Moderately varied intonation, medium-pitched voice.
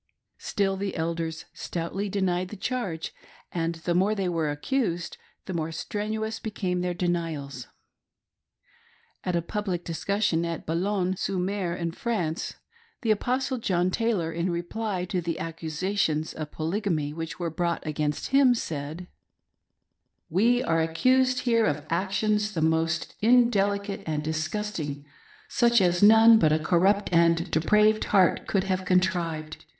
Yes: average, 4.2 semitones; medium, 180 Hz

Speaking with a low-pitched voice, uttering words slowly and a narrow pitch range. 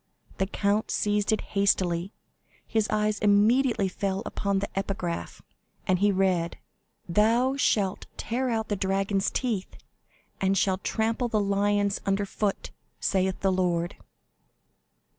No: high, 200 Hz; slow, 125 wpm; narrow, 1.9 semitones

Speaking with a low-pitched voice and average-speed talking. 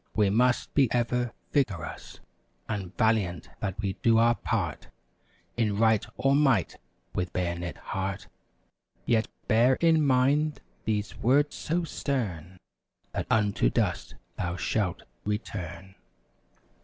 No: low, 110 Hz; slow, 120 wpm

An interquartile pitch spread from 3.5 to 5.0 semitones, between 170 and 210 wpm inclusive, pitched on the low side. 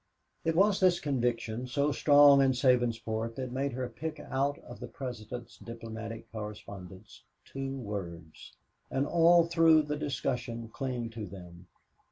No: average, 4.1 semitones; average, 140 wpm; low, 125 Hz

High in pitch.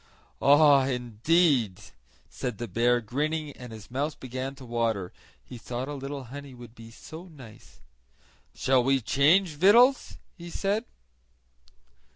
No: low, 135 Hz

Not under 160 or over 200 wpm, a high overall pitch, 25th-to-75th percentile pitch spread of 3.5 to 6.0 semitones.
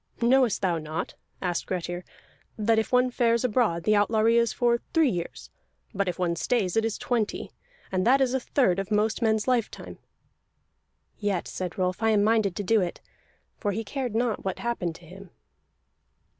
Yes: average, 180 wpm; high, 215 Hz; average, 4.3 semitones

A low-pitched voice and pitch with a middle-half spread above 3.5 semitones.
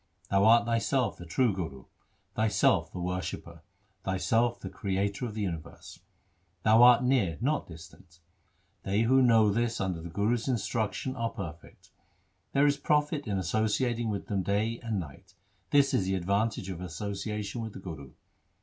Yes: low, 105 Hz; average, 3.9 semitones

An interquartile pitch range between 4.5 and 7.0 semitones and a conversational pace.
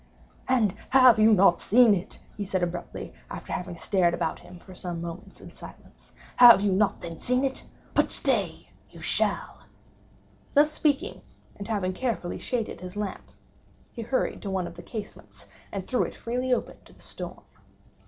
Yes: average, 5.3 semitones; average, 165 wpm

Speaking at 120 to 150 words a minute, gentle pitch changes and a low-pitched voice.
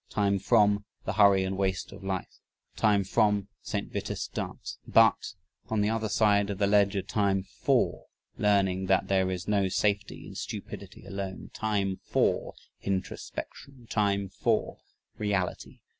Yes: average, 145 wpm; narrow, 1.4 semitones; low, 100 Hz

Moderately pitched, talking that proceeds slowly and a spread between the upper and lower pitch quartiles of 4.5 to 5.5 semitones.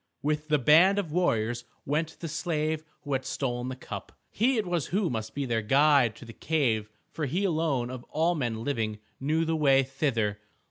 No: medium, 145 Hz; average, 195 wpm; average, 4.9 semitones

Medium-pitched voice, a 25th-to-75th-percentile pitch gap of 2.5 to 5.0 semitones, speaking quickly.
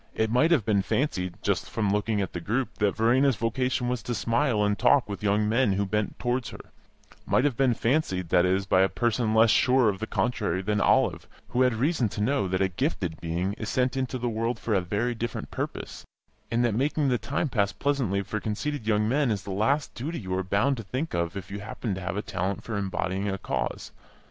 No: low, 110 Hz; average, 4.2 semitones; fast, 230 wpm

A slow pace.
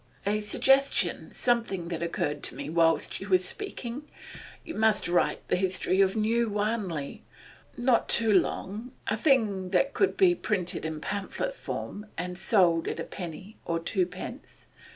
No: average, 150 wpm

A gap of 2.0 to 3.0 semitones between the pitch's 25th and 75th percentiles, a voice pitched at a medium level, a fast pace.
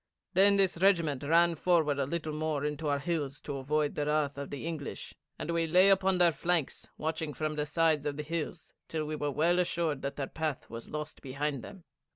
Yes: narrow, 2.6 semitones; medium, 155 Hz; fast, 210 wpm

